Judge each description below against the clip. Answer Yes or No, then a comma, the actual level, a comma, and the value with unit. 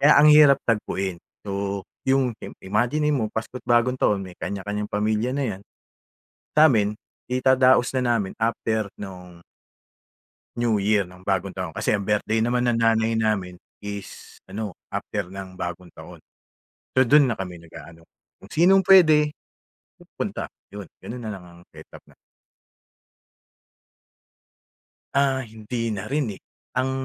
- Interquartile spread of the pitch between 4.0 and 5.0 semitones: Yes, average, 4.4 semitones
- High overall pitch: No, low, 110 Hz